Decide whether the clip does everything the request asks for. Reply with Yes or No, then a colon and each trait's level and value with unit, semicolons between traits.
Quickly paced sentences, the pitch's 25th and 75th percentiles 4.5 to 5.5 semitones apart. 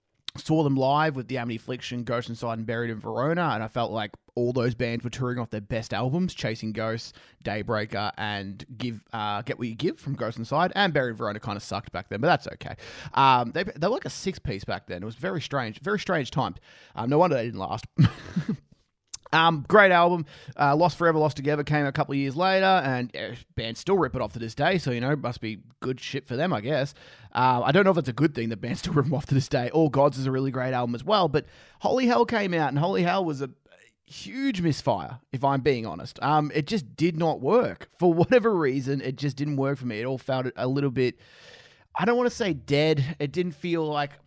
Yes: fast, 245 wpm; average, 5.1 semitones